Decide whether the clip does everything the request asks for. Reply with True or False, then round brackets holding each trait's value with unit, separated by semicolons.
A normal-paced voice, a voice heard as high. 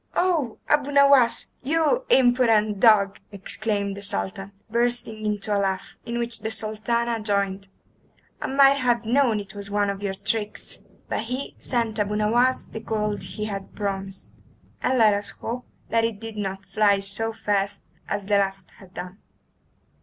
True (160 wpm; 215 Hz)